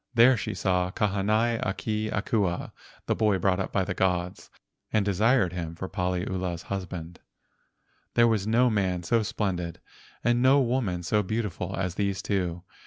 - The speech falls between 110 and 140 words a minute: No, average, 160 wpm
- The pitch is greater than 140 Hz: No, very low, 95 Hz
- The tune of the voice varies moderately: Yes, average, 3.3 semitones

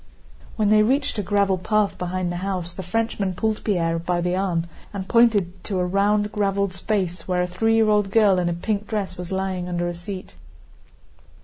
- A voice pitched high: Yes, high, 195 Hz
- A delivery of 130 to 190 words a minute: No, average, 200 wpm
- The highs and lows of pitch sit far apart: No, average, 2.7 semitones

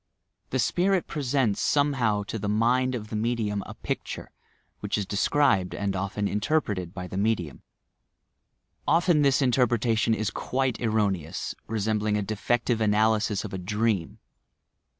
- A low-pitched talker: Yes, low, 110 Hz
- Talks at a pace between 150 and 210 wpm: No, average, 140 wpm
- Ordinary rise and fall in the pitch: Yes, average, 3.5 semitones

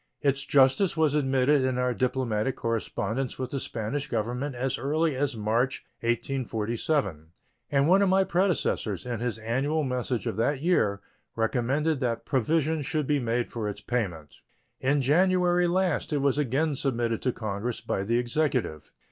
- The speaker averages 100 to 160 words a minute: Yes, average, 155 wpm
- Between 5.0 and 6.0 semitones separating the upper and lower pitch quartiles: No, average, 4.2 semitones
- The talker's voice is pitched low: Yes, low, 130 Hz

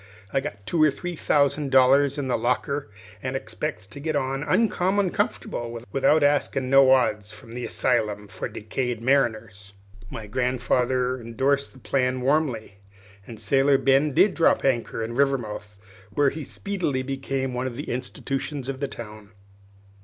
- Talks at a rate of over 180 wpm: No, average, 155 wpm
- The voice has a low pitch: Yes, low, 130 Hz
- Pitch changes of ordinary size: Yes, average, 3.3 semitones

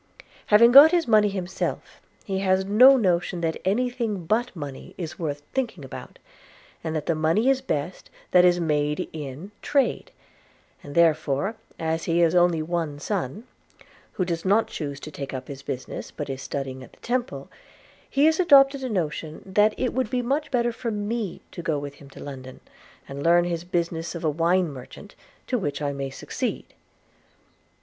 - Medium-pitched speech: Yes, medium, 175 Hz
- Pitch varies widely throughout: Yes, wide, 6.9 semitones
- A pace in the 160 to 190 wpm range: Yes, average, 180 wpm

